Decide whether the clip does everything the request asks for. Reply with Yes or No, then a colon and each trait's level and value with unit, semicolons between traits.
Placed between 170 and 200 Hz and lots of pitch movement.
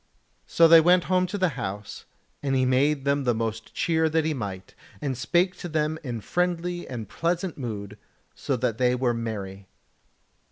No: low, 135 Hz; wide, 6.3 semitones